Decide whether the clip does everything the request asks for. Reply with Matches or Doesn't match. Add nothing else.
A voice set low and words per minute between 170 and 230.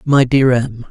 Matches